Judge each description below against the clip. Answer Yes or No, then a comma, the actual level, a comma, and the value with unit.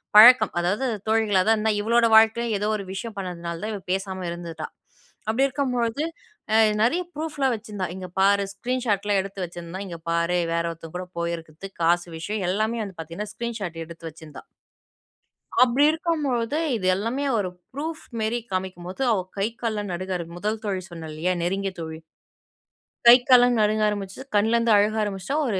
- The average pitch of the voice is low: No, high, 205 Hz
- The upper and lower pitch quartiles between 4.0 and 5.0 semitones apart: Yes, average, 4.4 semitones